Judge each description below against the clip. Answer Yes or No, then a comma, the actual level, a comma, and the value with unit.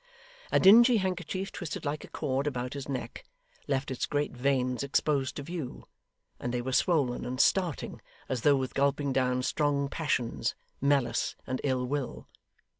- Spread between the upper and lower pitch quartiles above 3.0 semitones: No, average, 2.7 semitones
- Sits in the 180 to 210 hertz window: No, medium, 140 Hz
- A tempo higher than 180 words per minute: No, average, 160 wpm